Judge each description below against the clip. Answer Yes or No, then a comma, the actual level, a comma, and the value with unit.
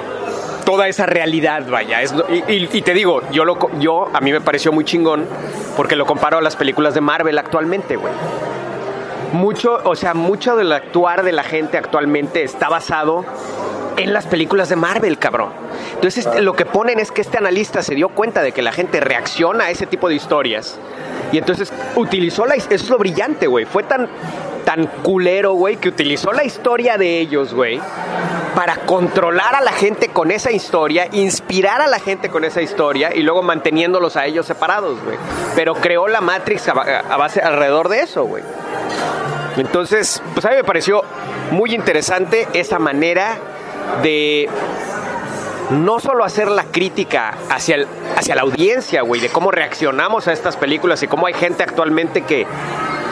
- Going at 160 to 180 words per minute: Yes, average, 175 wpm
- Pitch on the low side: No, medium, 175 Hz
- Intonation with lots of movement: No, average, 3.8 semitones